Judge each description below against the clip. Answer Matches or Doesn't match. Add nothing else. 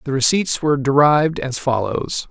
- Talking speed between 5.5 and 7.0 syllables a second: Doesn't match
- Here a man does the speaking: Matches